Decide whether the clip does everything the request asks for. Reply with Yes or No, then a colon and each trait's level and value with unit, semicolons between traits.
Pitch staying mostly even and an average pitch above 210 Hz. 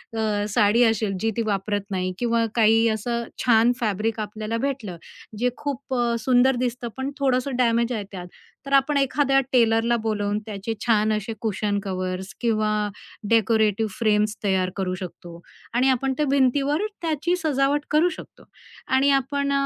No: average, 4.0 semitones; high, 230 Hz